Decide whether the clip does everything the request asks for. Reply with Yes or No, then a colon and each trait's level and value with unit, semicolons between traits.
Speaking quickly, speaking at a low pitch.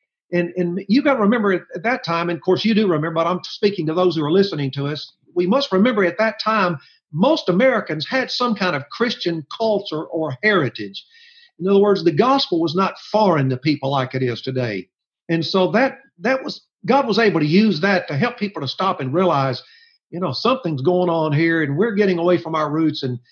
No: fast, 225 wpm; medium, 180 Hz